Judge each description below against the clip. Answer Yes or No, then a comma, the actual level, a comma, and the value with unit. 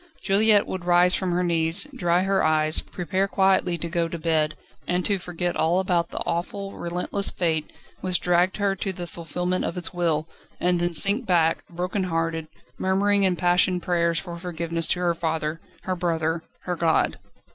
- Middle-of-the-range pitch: Yes, medium, 175 Hz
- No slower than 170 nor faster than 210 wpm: Yes, average, 175 wpm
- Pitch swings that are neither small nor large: No, narrow, 1.9 semitones